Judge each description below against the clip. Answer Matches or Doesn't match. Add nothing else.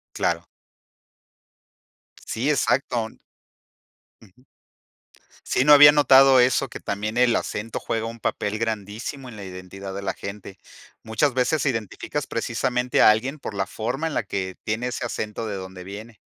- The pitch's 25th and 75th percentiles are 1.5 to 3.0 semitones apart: Doesn't match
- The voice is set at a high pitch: Doesn't match